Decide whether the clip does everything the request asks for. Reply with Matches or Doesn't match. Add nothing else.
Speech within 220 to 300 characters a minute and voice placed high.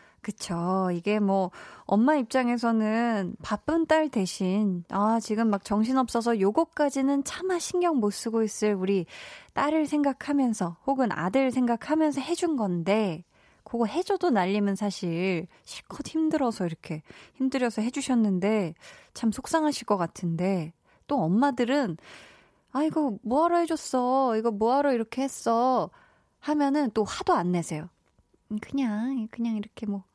Matches